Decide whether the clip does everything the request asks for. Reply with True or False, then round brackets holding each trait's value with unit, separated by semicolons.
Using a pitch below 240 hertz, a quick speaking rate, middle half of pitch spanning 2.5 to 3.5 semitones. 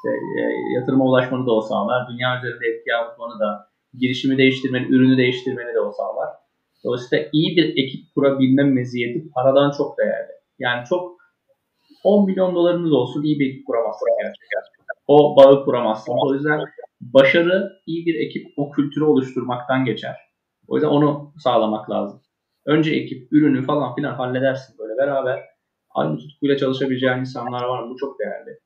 True (135 Hz; 155 wpm; 3.2 semitones)